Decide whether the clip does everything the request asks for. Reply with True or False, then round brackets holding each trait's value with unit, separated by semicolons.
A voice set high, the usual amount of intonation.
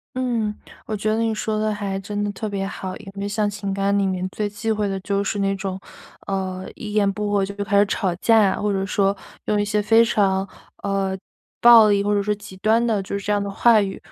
False (205 Hz; 1.5 semitones)